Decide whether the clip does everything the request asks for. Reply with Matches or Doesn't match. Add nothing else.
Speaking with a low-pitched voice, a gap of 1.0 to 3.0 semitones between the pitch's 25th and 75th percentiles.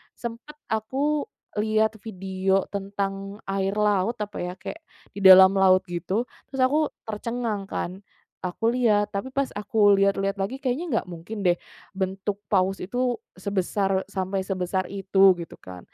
Doesn't match